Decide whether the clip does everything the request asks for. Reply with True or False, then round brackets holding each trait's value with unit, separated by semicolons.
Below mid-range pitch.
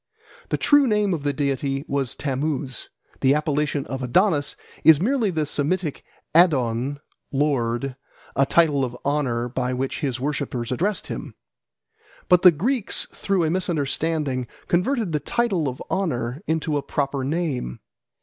False (145 Hz)